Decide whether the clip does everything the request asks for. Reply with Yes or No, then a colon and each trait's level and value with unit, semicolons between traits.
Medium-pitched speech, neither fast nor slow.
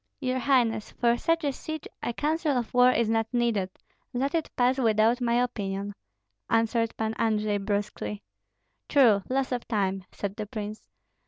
No: high, 230 Hz; average, 160 wpm